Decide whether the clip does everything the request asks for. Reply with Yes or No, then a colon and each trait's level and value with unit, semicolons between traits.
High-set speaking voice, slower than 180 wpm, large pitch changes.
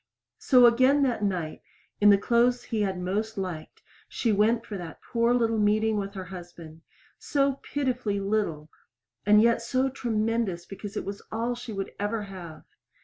No: high, 215 Hz; average, 165 wpm; average, 3.4 semitones